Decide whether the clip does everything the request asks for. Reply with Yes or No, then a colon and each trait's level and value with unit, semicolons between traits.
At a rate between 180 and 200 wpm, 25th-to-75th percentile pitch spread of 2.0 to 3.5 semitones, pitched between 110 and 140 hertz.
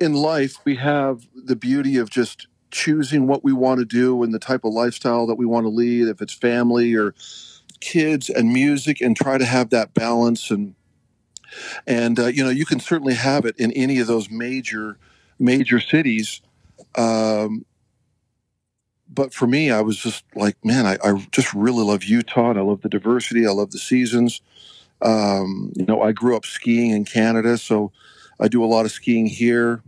Yes: average, 190 wpm; narrow, 2.5 semitones; low, 120 Hz